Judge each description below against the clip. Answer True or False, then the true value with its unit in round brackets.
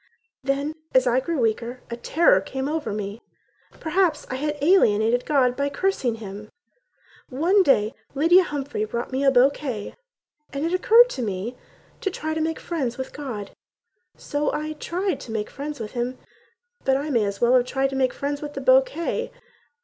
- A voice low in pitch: False (270 Hz)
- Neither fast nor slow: True (180 wpm)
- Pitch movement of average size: True (4.7 semitones)